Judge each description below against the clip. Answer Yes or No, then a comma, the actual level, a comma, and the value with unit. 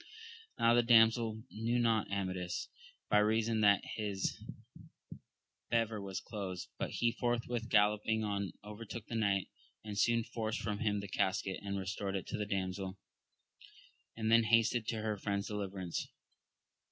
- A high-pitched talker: No, low, 105 Hz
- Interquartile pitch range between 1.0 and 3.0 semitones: Yes, narrow, 2.4 semitones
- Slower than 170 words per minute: Yes, average, 145 wpm